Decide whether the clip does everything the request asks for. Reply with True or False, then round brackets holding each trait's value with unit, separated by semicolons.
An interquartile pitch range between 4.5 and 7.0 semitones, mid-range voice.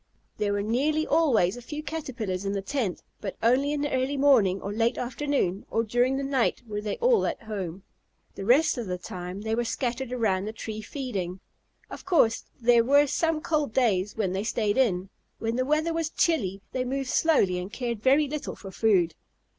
False (5.6 semitones; 235 Hz)